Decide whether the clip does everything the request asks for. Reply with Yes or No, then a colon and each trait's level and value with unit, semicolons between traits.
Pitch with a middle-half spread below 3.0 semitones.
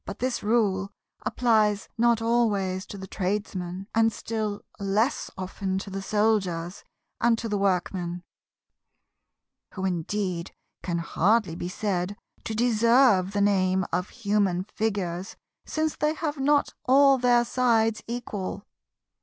No: average, 3.5 semitones